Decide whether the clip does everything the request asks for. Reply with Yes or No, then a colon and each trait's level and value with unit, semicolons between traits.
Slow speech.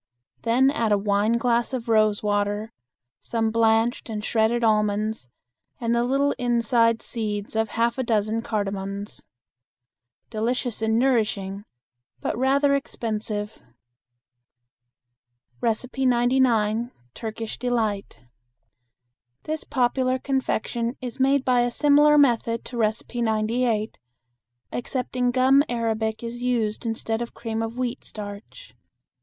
Yes: slow, 110 wpm